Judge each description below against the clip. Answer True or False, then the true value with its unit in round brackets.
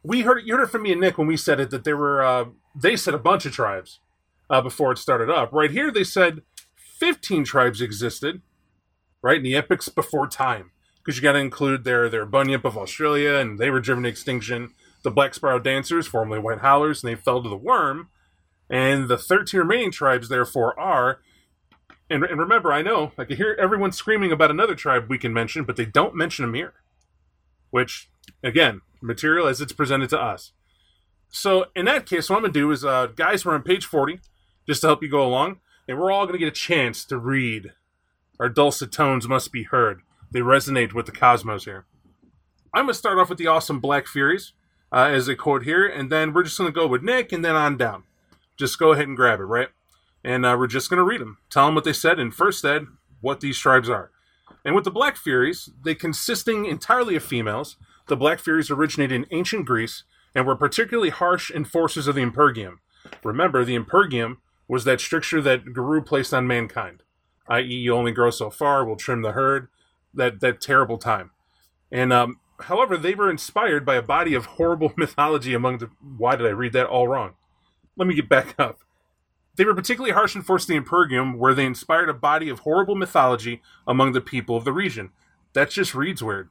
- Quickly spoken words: True (210 wpm)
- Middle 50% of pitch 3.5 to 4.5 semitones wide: False (4.9 semitones)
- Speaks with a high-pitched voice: False (135 Hz)